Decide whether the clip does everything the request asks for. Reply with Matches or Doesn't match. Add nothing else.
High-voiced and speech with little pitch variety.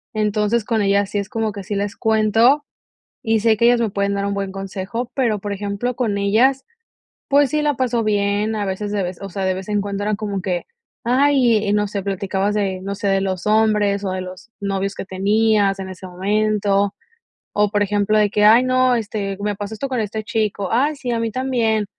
Matches